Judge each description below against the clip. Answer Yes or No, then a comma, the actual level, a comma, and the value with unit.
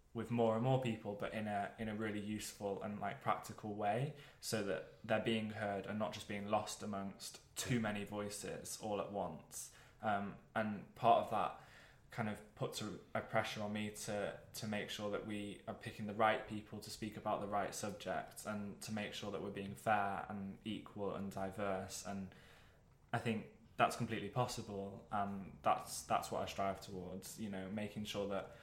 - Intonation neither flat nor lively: No, narrow, 1.6 semitones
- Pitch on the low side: Yes, low, 105 Hz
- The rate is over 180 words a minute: Yes, average, 195 wpm